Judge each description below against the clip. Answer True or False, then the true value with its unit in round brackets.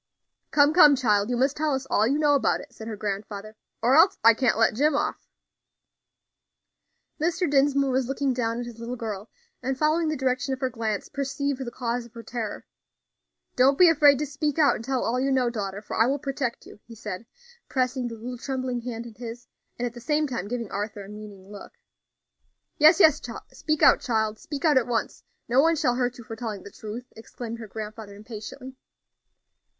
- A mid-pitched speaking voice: False (245 Hz)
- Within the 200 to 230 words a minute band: True (205 wpm)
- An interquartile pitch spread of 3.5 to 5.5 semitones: True (3.8 semitones)